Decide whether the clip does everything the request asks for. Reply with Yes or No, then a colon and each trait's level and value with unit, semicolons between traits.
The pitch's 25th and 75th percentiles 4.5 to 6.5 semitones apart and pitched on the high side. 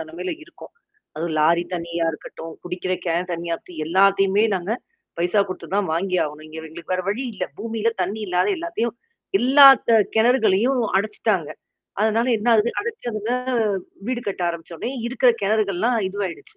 Yes: average, 4.8 semitones; high, 195 Hz